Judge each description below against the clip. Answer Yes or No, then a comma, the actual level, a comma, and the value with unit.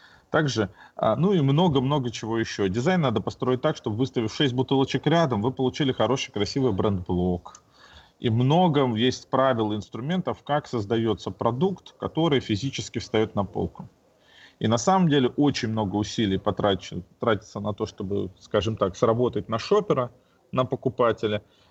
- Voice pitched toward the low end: Yes, low, 120 Hz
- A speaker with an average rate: Yes, average, 145 wpm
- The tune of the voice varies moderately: Yes, average, 4.2 semitones